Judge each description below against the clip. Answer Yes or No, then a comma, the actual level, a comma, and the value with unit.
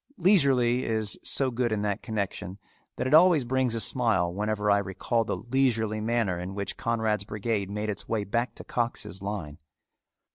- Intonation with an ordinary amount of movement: Yes, average, 3.0 semitones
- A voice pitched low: Yes, low, 110 Hz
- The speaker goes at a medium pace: Yes, average, 175 wpm